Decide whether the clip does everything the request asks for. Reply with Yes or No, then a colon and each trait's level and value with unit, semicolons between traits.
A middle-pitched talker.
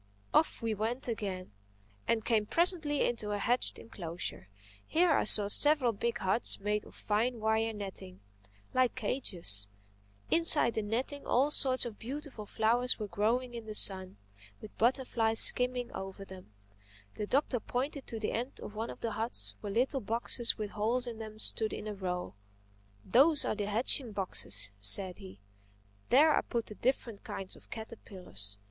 No: high, 225 Hz